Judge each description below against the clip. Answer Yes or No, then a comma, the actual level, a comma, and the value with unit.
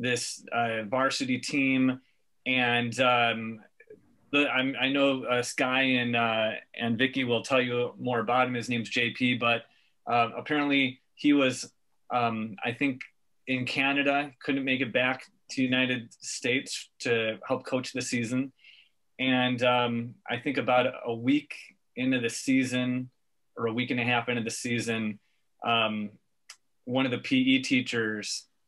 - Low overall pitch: Yes, low, 125 Hz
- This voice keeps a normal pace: Yes, average, 150 wpm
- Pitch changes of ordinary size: No, narrow, 1.9 semitones